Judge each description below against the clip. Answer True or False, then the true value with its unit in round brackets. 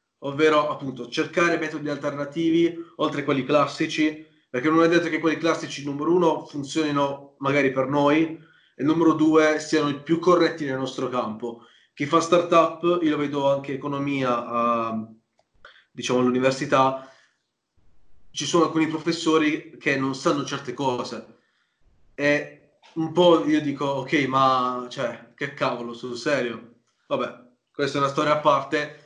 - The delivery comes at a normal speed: True (150 wpm)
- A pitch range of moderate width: True (3.0 semitones)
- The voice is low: False (145 Hz)